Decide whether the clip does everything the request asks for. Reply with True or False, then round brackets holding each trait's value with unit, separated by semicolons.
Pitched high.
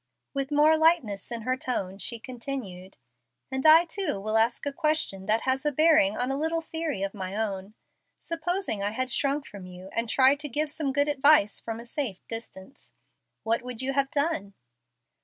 True (260 Hz)